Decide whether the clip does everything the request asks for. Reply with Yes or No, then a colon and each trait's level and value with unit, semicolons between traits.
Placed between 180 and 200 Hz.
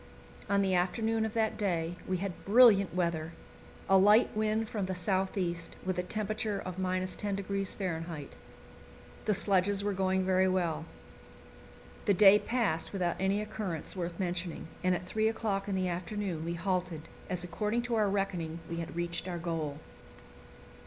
Yes: medium, 185 Hz